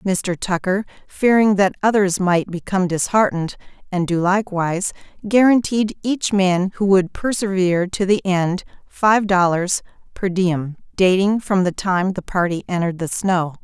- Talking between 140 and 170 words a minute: Yes, average, 145 wpm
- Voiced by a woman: Yes, female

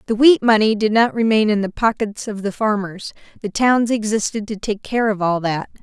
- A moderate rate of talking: No, fast, 215 wpm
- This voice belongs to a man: No, female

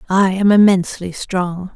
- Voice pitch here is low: No, medium, 185 Hz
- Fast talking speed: No, slow, 135 wpm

